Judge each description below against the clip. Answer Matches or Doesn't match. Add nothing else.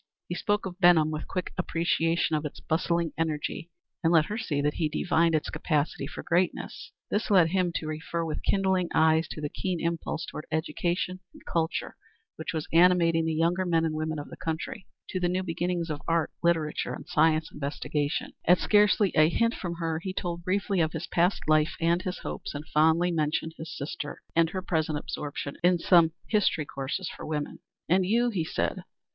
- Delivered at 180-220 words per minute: Matches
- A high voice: Doesn't match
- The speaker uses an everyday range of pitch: Doesn't match